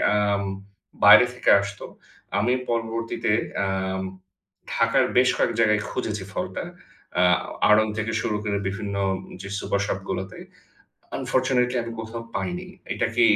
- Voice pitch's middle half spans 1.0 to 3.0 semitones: Yes, average, 2.7 semitones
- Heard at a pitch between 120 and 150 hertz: No, low, 105 Hz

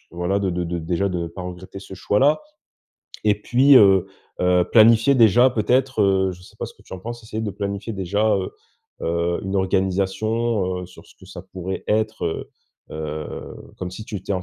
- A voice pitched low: Yes, very low, 95 Hz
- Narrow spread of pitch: No, average, 3.3 semitones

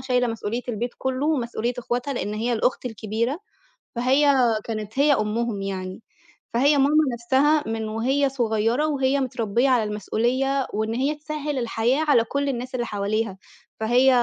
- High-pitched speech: Yes, high, 245 Hz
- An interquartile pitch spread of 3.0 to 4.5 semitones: Yes, average, 3.4 semitones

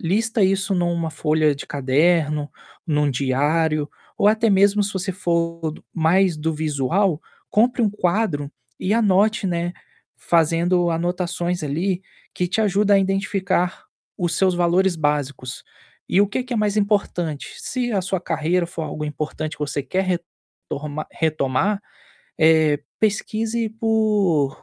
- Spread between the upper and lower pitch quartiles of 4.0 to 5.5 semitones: Yes, average, 4.3 semitones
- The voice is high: No, medium, 175 Hz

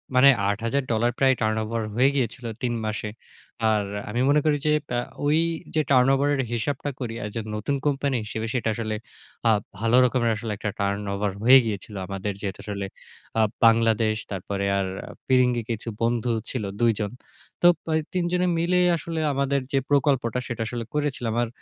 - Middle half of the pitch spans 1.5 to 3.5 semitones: No, average, 4.0 semitones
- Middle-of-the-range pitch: No, low, 120 Hz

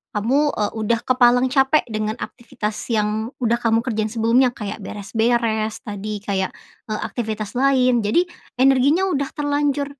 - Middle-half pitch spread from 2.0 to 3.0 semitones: No, average, 3.7 semitones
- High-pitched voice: Yes, high, 235 Hz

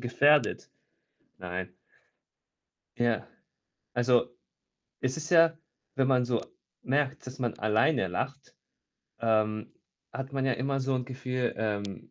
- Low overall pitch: Yes, low, 125 Hz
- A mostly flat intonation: No, average, 3.5 semitones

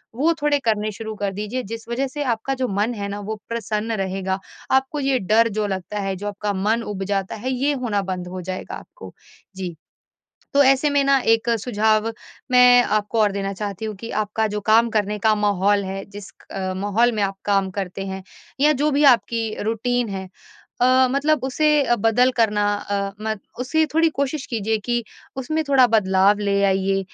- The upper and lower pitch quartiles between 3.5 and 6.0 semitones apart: Yes, average, 4.0 semitones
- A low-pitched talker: No, high, 215 Hz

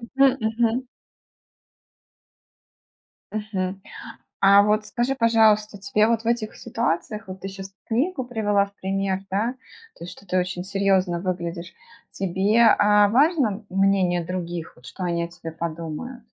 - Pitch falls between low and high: No, high, 200 Hz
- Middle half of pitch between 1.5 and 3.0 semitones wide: No, average, 3.4 semitones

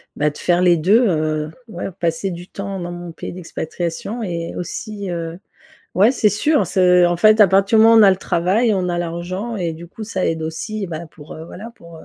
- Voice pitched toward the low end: No, medium, 180 Hz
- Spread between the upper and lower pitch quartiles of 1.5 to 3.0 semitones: No, average, 3.5 semitones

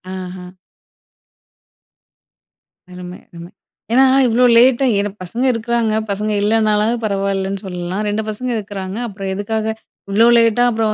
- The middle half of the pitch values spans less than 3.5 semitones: Yes, average, 2.9 semitones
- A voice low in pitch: No, high, 210 Hz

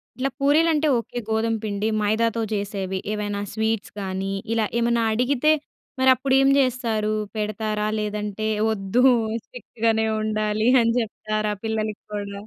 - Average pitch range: No, narrow, 1.9 semitones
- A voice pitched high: Yes, high, 220 Hz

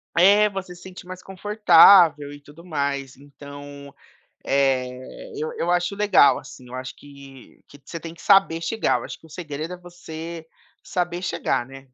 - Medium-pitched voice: Yes, medium, 165 Hz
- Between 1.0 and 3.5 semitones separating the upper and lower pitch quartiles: No, average, 4.3 semitones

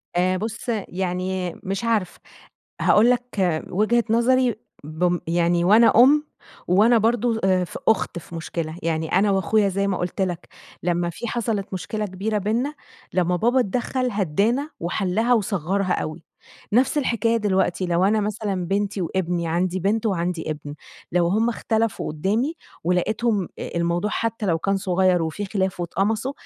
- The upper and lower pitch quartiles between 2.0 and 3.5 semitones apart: No, average, 4.1 semitones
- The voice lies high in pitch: Yes, high, 195 Hz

